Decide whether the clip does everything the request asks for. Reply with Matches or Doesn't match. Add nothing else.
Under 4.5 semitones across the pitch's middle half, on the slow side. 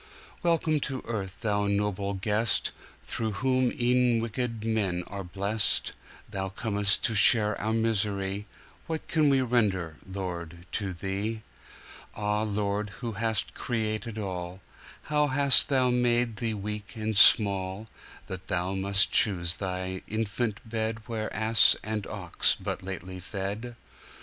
Matches